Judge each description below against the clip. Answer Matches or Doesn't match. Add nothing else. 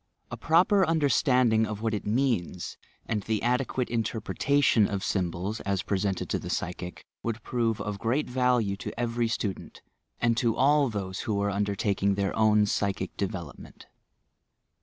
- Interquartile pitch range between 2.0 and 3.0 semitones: Doesn't match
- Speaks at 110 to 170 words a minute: Matches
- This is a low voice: Matches